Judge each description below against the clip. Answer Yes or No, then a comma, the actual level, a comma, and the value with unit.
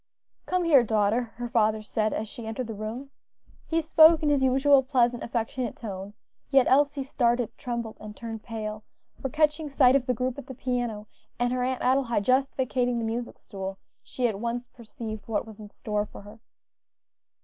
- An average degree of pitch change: Yes, average, 3.2 semitones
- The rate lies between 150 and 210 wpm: Yes, average, 185 wpm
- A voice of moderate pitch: No, high, 240 Hz